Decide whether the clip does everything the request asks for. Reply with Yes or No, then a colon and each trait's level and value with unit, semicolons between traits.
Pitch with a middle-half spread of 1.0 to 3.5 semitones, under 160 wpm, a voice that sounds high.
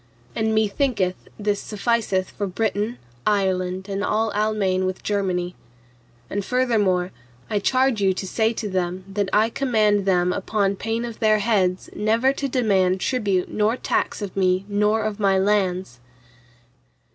Yes: average, 2.7 semitones; average, 145 wpm; high, 205 Hz